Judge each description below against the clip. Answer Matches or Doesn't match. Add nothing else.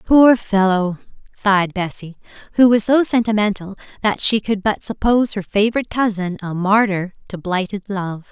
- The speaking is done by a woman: Matches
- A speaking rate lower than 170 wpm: Matches